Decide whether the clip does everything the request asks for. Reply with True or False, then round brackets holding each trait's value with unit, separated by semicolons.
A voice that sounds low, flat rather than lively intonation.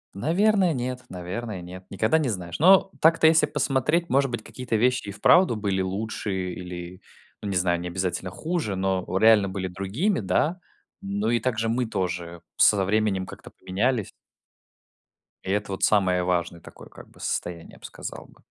False (100 Hz; 5.5 semitones)